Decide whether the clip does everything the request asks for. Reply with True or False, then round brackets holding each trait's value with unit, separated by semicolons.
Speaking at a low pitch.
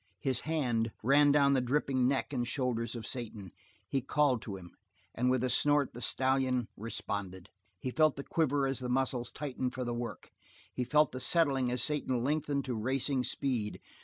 True (130 Hz)